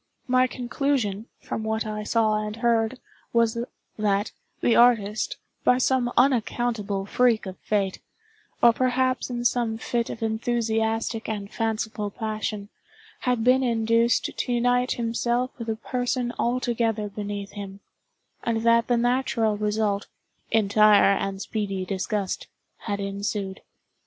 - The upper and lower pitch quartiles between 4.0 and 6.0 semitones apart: No, narrow, 2.5 semitones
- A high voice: Yes, high, 225 Hz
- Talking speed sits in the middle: No, slow, 125 wpm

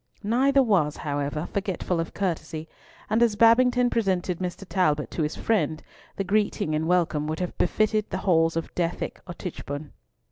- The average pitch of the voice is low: No, medium, 180 Hz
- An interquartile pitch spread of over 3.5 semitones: Yes, average, 5.1 semitones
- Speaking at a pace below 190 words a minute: Yes, average, 165 wpm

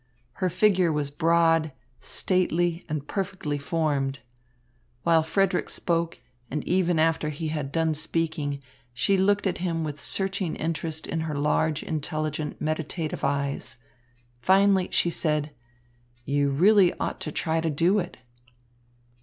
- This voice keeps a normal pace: No, slow, 130 wpm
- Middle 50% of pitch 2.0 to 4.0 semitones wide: Yes, average, 2.8 semitones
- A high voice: No, medium, 160 Hz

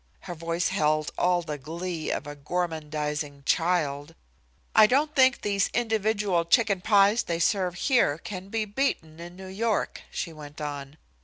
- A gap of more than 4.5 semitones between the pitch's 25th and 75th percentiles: Yes, average, 5.1 semitones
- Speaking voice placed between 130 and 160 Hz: No, medium, 175 Hz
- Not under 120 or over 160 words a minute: Yes, average, 155 wpm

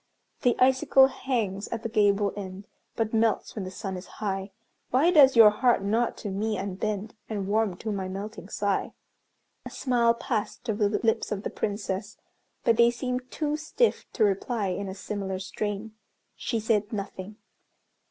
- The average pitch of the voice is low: No, high, 215 Hz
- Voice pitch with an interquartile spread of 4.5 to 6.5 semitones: No, average, 2.9 semitones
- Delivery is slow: No, average, 170 wpm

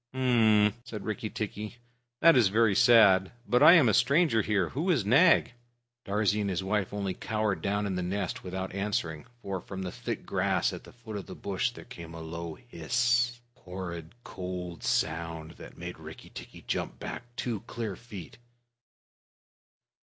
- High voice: No, low, 105 Hz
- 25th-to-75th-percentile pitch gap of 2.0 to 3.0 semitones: No, average, 4.2 semitones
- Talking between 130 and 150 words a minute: No, average, 175 wpm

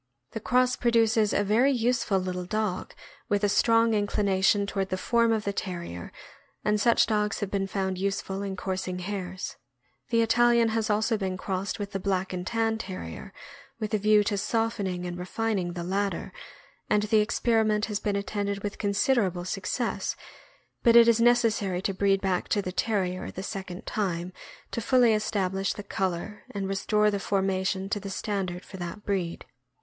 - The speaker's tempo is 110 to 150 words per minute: No, average, 175 wpm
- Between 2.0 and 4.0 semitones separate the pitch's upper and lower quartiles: Yes, narrow, 2.6 semitones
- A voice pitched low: No, high, 200 Hz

